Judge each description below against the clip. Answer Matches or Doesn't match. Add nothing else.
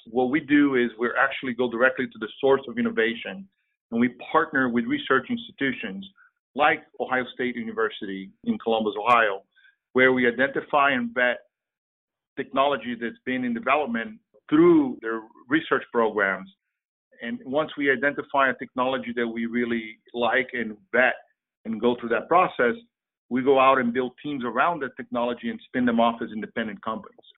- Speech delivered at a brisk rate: Doesn't match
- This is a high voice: Doesn't match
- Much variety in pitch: Doesn't match